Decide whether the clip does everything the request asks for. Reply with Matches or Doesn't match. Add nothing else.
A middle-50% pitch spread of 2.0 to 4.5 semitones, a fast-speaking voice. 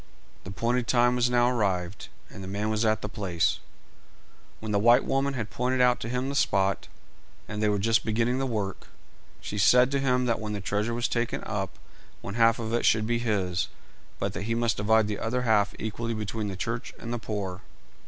Matches